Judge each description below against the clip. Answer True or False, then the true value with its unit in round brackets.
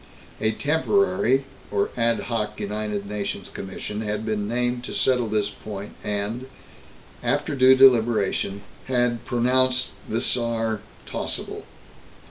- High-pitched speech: False (115 Hz)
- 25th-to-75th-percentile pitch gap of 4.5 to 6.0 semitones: False (3.3 semitones)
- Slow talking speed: True (115 wpm)